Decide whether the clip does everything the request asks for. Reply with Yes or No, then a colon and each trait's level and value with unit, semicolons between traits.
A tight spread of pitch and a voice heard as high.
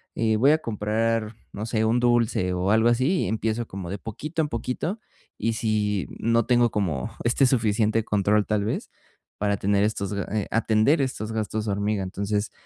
No: narrow, 2.3 semitones; low, 110 Hz